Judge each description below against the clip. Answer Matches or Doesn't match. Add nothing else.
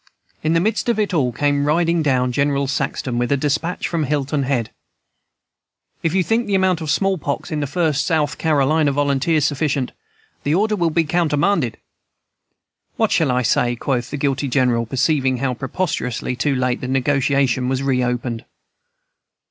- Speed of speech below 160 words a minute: Doesn't match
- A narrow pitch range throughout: Doesn't match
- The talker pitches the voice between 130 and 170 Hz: Matches